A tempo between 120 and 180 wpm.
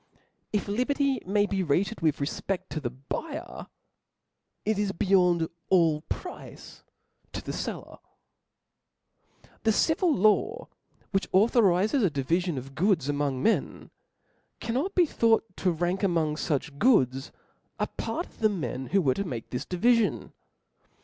Yes: slow, 135 wpm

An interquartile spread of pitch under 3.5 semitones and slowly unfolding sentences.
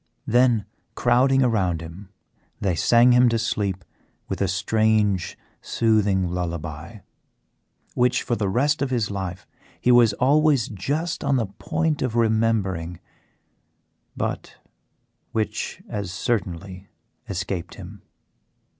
No: average, 4.6 semitones; slow, 115 wpm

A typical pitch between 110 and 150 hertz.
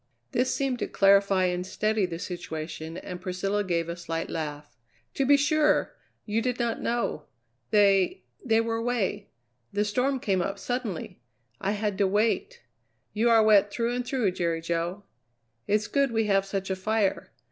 No: high, 205 Hz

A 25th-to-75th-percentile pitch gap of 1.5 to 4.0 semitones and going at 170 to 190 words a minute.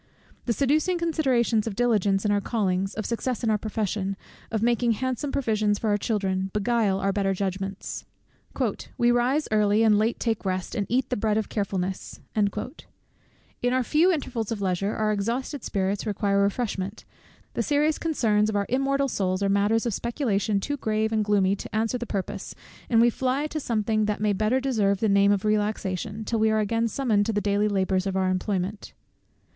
Yes: average, 3.1 semitones; average, 185 wpm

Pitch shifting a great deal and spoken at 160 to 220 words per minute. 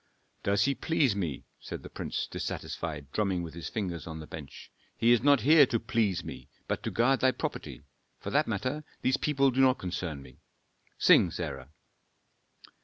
Yes: wide, 8.1 semitones; average, 180 wpm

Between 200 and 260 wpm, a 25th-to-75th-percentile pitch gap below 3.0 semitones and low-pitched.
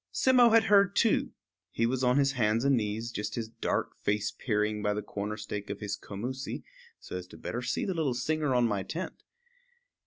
No: fast, 205 wpm; average, 4.9 semitones; low, 115 Hz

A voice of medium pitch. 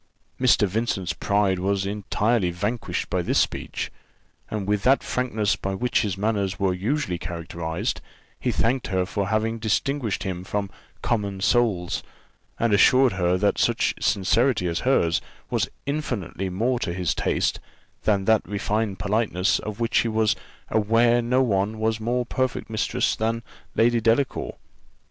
No: low, 105 Hz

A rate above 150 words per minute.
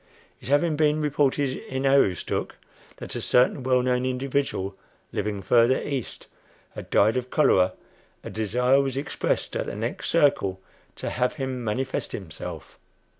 No: average, 145 wpm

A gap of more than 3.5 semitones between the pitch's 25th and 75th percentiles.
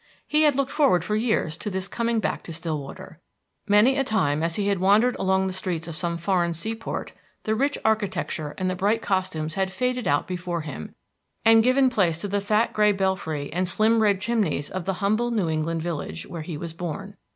Yes: average, 4.6 semitones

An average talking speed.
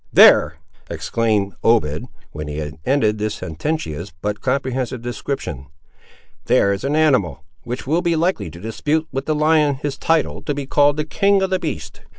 Yes: average, 170 wpm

